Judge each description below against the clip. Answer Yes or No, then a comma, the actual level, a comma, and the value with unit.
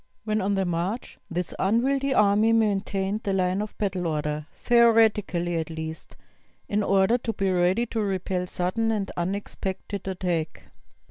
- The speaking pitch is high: Yes, high, 195 Hz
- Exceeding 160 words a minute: No, average, 145 wpm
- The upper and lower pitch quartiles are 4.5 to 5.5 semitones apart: No, average, 3.3 semitones